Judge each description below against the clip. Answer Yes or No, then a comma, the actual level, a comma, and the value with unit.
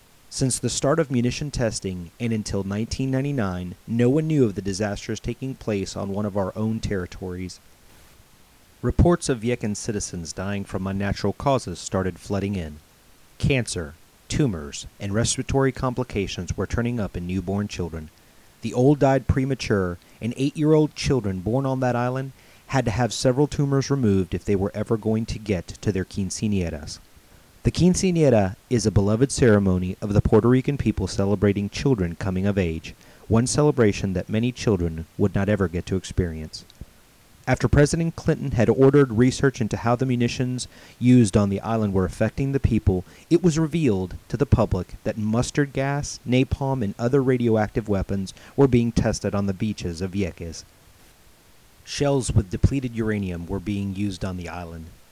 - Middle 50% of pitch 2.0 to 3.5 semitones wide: No, average, 4.9 semitones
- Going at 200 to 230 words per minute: No, average, 160 wpm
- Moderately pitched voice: No, low, 110 Hz